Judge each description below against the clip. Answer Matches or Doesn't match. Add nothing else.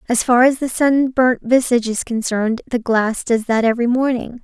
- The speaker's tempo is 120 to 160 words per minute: Doesn't match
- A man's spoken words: Doesn't match